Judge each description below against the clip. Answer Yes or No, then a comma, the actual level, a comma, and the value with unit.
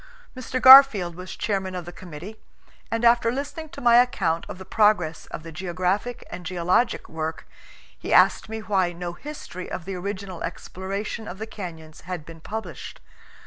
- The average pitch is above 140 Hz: Yes, high, 190 Hz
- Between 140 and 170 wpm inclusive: No, average, 180 wpm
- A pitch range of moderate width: Yes, average, 4.2 semitones